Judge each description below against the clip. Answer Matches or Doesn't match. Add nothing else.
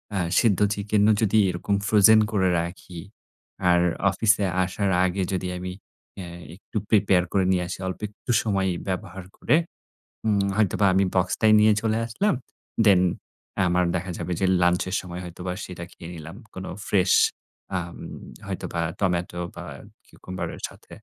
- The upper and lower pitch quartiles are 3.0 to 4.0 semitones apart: Doesn't match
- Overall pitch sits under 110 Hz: Matches